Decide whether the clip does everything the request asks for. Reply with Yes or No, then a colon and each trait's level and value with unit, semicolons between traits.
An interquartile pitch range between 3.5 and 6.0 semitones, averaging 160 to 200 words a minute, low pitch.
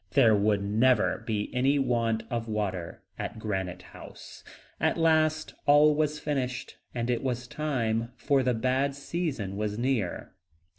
No: average, 4.6 semitones; average, 145 wpm; low, 120 Hz